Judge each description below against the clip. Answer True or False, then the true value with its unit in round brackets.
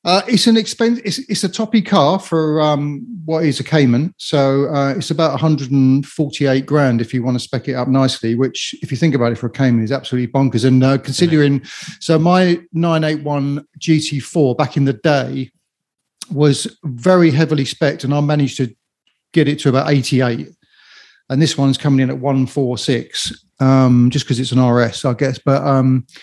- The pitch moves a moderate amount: True (3.3 semitones)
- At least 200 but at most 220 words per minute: False (190 wpm)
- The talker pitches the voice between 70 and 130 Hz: False (140 Hz)